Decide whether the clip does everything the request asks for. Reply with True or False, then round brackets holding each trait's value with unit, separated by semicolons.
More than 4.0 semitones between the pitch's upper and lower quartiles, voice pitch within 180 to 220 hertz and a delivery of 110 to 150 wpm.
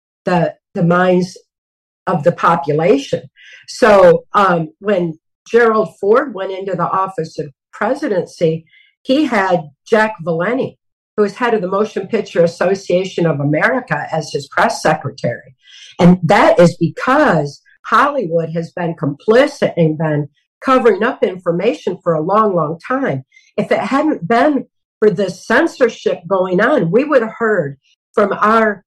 True (5.1 semitones; 190 Hz; 140 wpm)